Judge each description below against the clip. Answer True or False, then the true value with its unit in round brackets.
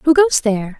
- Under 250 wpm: True (225 wpm)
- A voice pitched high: True (265 Hz)